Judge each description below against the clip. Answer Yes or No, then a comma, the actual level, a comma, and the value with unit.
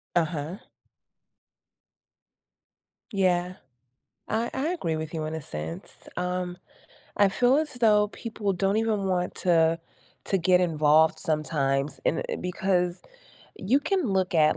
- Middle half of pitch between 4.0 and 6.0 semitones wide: Yes, average, 4.5 semitones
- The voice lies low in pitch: No, medium, 180 Hz